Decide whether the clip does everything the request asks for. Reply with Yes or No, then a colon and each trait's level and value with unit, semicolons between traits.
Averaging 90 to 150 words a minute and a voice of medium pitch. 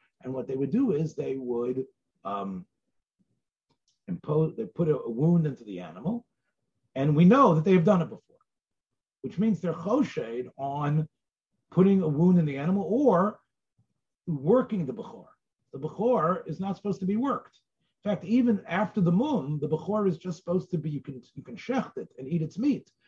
No: average, 185 wpm; medium, 170 Hz